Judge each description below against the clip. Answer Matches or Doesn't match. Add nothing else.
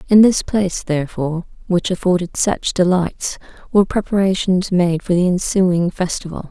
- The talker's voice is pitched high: Doesn't match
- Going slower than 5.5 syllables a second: Matches